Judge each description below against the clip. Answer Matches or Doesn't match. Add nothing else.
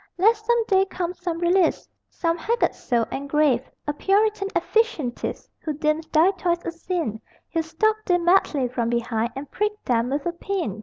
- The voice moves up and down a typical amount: Doesn't match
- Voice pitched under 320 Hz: Doesn't match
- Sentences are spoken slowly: Doesn't match